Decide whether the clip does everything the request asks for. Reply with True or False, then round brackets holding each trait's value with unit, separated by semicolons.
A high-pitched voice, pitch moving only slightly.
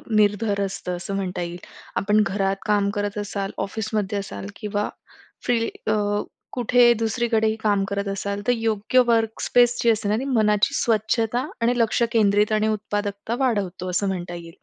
True (210 Hz; 2.2 semitones)